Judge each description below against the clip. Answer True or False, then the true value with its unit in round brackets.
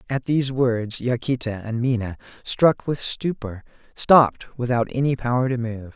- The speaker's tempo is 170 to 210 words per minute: False (150 wpm)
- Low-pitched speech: True (125 Hz)